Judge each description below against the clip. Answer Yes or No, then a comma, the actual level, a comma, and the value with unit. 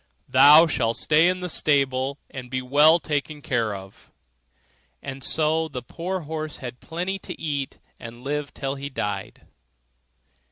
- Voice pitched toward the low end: No, medium, 145 Hz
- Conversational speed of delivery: Yes, average, 155 wpm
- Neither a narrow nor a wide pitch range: Yes, average, 3.6 semitones